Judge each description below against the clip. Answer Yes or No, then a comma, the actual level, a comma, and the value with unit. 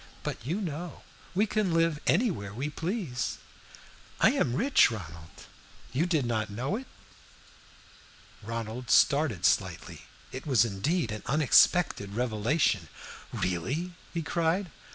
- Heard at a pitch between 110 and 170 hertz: Yes, medium, 140 Hz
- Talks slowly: Yes, slow, 120 wpm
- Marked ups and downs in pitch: Yes, wide, 7.5 semitones